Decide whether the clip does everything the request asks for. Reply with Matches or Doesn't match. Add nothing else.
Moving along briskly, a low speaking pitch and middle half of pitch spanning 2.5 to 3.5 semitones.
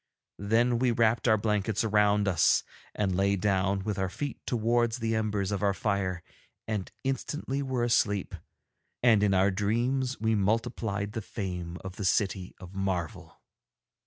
Doesn't match